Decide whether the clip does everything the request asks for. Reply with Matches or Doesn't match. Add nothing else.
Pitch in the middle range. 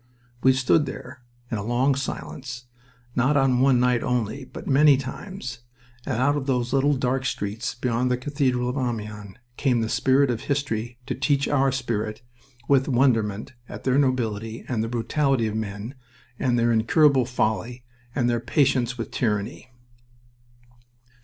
Doesn't match